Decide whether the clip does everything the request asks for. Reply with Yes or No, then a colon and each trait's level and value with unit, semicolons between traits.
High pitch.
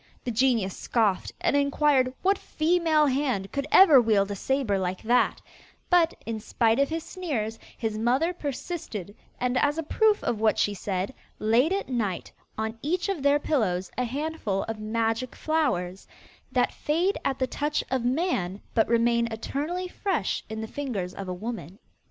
Yes: high, 245 Hz